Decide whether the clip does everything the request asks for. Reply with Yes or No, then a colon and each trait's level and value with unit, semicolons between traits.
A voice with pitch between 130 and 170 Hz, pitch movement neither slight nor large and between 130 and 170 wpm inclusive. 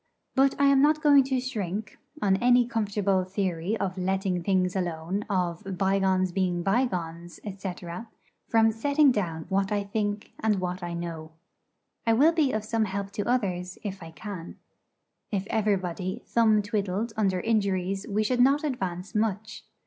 No: high, 200 Hz; average, 3.4 semitones; average, 155 wpm